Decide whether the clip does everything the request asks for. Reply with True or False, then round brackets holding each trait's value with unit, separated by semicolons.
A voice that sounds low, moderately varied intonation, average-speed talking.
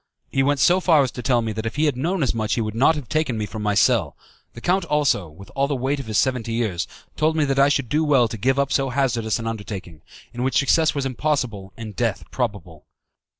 False (125 Hz; 4.4 semitones; 255 wpm)